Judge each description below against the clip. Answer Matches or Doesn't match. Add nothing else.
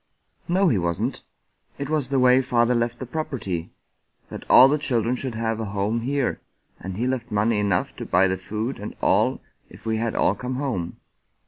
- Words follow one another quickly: Matches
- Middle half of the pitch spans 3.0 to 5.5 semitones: Matches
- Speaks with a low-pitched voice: Matches